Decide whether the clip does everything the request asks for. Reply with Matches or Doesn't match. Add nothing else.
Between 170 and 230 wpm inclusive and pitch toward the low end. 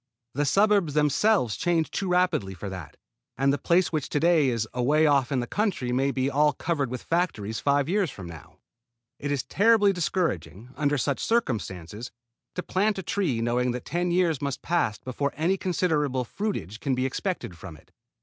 Doesn't match